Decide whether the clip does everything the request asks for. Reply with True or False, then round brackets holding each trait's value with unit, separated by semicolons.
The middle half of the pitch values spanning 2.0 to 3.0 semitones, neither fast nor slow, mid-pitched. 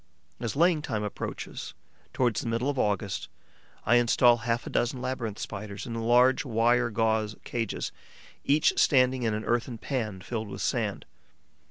False (2.5 semitones; 155 wpm; 115 Hz)